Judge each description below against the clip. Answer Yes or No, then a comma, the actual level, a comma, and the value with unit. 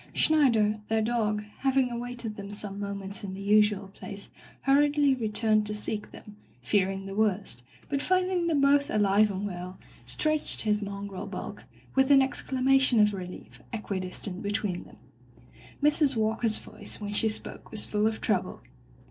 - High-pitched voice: Yes, high, 215 Hz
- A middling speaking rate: Yes, average, 155 wpm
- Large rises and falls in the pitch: No, average, 4.6 semitones